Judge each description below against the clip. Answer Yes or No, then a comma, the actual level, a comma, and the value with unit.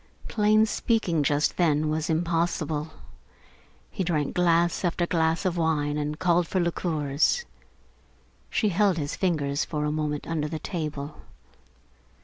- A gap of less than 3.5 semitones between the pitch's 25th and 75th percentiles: Yes, average, 2.7 semitones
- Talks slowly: Yes, slow, 130 wpm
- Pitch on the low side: No, medium, 160 Hz